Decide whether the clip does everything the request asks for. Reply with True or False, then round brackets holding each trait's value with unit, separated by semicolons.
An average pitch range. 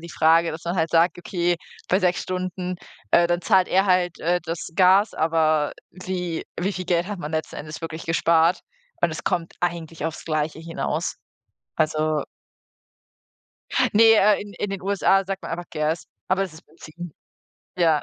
False (2.3 semitones)